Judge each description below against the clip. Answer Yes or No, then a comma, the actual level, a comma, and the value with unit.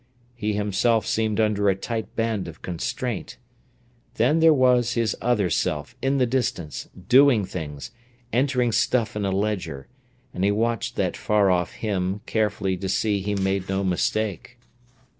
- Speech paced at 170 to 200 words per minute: No, average, 155 wpm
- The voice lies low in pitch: Yes, low, 105 Hz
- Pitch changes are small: No, average, 3.6 semitones